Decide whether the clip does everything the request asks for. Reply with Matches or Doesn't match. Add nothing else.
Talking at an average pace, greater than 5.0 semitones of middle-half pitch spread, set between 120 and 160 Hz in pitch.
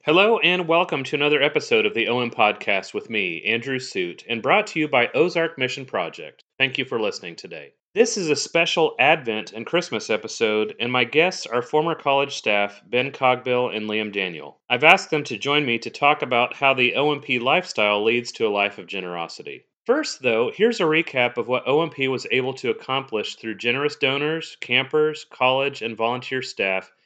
Matches